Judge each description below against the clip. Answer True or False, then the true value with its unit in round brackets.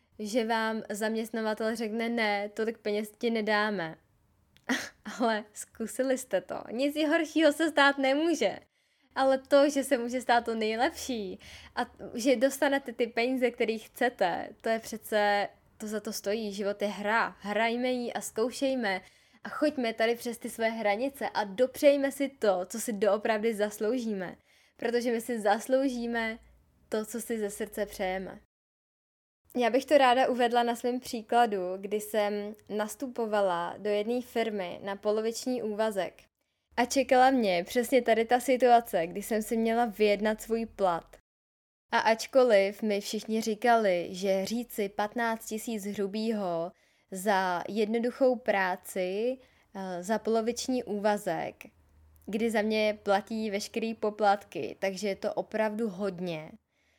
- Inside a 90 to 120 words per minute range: False (135 wpm)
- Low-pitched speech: False (220 Hz)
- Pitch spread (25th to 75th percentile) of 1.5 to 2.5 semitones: False (2.9 semitones)